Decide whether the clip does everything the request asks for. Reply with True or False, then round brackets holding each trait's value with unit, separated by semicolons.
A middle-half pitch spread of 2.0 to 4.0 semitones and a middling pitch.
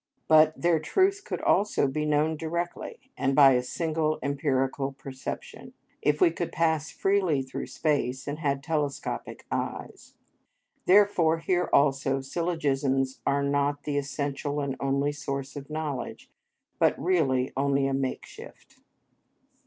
True (2.7 semitones; 145 Hz)